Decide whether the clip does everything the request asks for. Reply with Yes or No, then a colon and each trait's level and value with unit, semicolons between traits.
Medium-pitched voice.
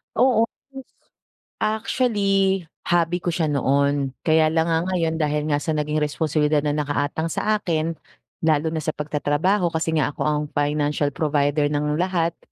Yes: medium, 155 Hz